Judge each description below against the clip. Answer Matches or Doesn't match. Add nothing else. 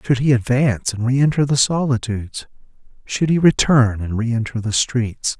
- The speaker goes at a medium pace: Matches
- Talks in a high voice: Doesn't match